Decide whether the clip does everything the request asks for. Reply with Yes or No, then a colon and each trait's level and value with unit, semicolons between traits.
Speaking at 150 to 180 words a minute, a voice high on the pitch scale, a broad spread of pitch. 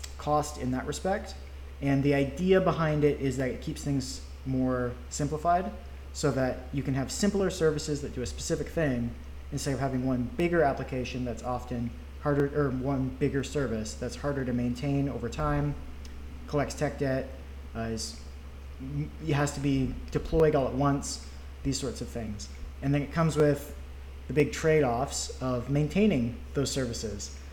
No: average, 170 wpm; low, 130 Hz; wide, 8.5 semitones